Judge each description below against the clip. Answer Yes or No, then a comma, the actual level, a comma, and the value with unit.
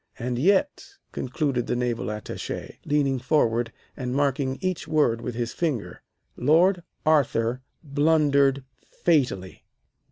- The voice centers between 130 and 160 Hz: Yes, low, 135 Hz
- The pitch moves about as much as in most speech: Yes, average, 4.0 semitones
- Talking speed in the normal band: No, slow, 115 wpm